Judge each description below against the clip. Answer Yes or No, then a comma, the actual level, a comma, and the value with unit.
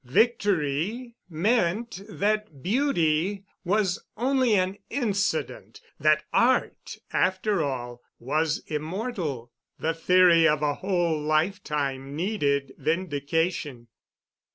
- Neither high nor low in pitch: Yes, medium, 170 Hz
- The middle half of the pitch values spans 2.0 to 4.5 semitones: No, wide, 5.5 semitones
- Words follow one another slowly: Yes, slow, 85 wpm